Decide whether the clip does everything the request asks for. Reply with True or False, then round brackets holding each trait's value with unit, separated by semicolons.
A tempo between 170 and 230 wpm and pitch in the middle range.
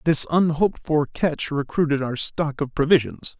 False (160 wpm; 150 Hz)